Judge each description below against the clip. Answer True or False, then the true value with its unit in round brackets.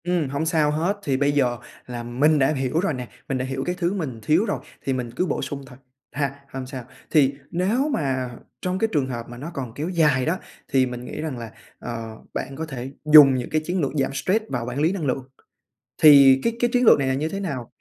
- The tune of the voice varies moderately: True (4.1 semitones)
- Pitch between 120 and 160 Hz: True (140 Hz)